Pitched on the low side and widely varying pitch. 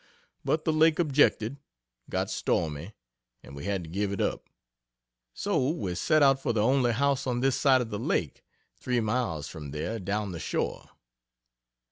Yes: low, 115 Hz; wide, 6.3 semitones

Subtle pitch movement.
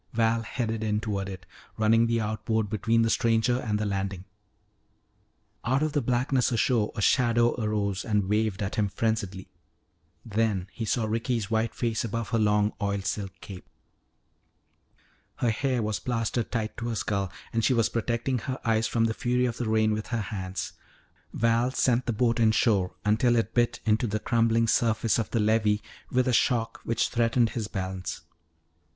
Yes: narrow, 2.0 semitones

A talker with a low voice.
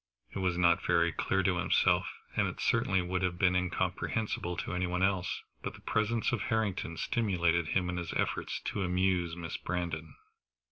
Yes: very low, 90 Hz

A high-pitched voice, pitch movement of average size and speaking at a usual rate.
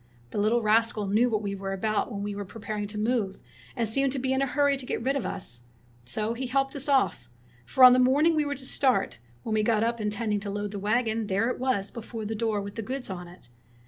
No: high, 225 Hz; average, 3.8 semitones; fast, 265 wpm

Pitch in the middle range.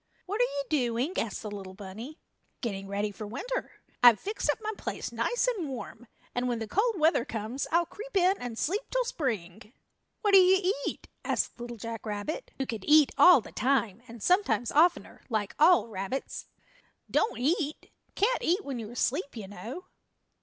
No: very high, 260 Hz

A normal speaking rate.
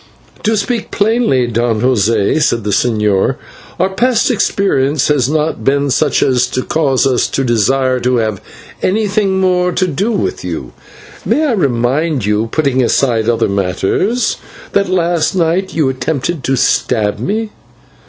Yes: average, 150 wpm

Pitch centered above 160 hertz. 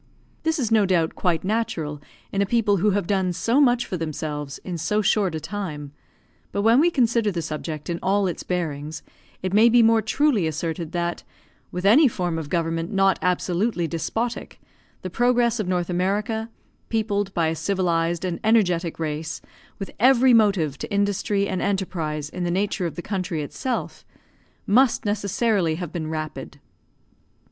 Yes: medium, 185 Hz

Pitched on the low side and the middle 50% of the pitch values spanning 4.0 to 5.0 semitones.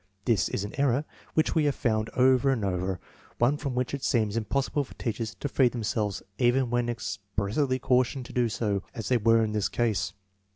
No: low, 120 Hz; average, 3.4 semitones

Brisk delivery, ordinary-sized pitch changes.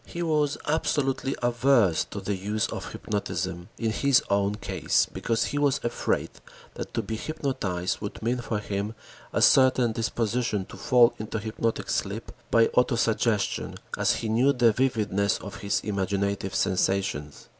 No: average, 155 wpm; average, 3.8 semitones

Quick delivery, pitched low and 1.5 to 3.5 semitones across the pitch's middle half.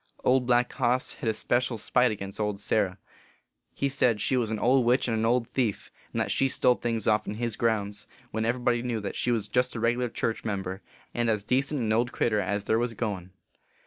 Yes: fast, 210 wpm; low, 115 Hz; average, 2.7 semitones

